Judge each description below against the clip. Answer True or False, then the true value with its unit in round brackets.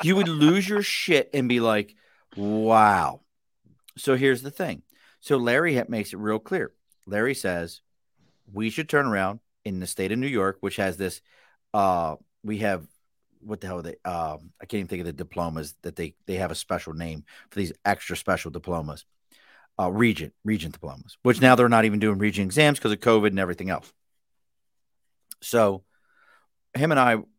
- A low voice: True (105 Hz)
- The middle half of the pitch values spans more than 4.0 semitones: True (5.2 semitones)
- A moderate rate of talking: True (185 wpm)